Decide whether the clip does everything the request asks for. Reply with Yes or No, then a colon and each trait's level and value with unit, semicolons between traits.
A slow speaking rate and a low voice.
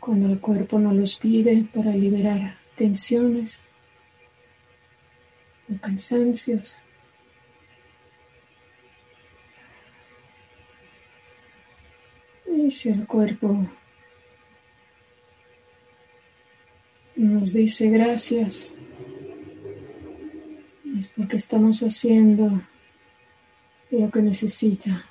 No: slow, 60 wpm; medium, 185 Hz